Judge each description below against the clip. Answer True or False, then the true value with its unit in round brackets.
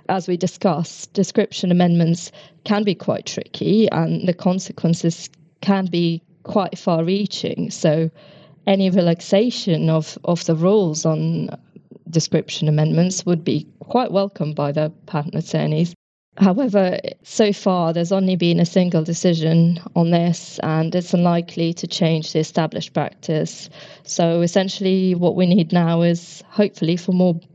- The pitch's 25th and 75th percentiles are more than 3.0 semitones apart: False (2.6 semitones)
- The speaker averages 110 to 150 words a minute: True (140 wpm)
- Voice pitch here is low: False (175 Hz)